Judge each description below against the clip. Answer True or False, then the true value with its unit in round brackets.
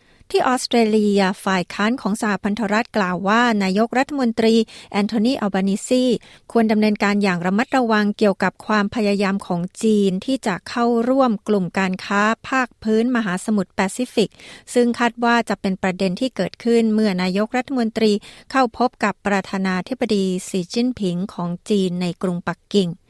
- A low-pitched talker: False (210 Hz)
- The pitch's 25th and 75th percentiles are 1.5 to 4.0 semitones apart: True (3.4 semitones)